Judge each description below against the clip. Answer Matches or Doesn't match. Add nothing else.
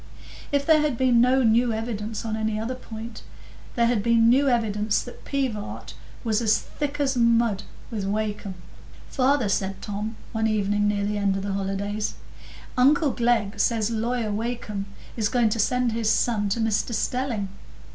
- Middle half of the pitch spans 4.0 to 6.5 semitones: Doesn't match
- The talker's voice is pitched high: Matches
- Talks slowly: Doesn't match